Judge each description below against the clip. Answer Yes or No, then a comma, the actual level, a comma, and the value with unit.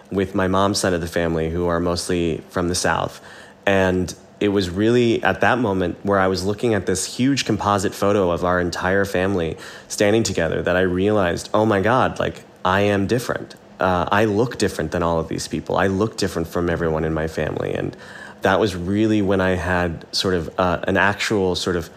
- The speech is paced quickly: Yes, fast, 210 wpm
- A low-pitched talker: Yes, very low, 95 Hz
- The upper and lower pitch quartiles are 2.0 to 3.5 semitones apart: Yes, narrow, 2.6 semitones